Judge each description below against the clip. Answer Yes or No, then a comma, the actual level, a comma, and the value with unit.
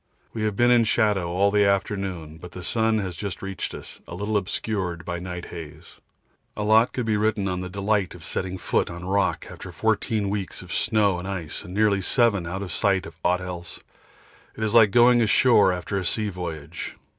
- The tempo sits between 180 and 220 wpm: Yes, fast, 205 wpm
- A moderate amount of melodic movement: Yes, average, 3.2 semitones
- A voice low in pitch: Yes, low, 100 Hz